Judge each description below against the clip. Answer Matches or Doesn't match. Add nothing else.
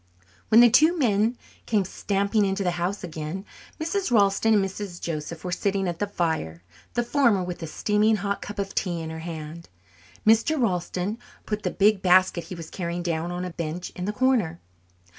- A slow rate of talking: Doesn't match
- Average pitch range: Matches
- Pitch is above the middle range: Matches